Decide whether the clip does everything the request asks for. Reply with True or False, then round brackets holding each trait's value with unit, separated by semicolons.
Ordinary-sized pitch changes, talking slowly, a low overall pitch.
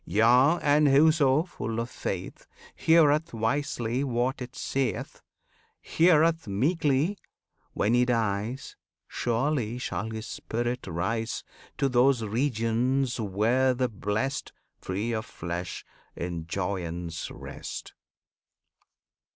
True (4.1 semitones; 100 wpm; 120 Hz)